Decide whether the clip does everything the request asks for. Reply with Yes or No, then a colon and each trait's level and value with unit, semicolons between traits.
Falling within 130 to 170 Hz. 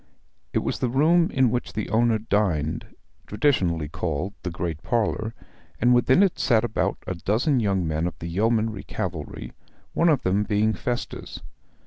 No: low, 110 Hz